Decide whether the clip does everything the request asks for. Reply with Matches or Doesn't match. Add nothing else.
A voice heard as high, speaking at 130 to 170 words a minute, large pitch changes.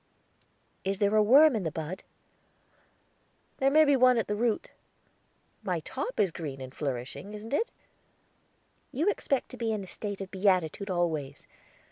Matches